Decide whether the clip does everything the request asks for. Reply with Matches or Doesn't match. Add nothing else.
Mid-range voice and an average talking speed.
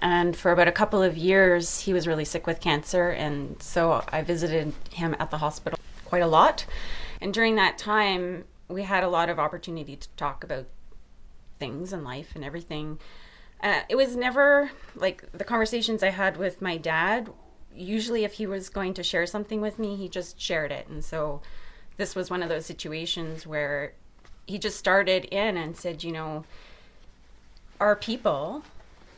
Matches